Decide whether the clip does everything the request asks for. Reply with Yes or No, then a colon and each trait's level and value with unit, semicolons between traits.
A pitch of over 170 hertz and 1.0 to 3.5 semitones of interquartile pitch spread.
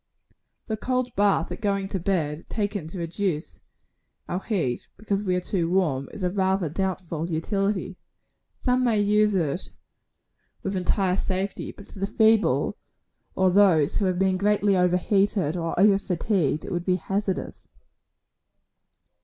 Yes: high, 190 Hz; narrow, 2.5 semitones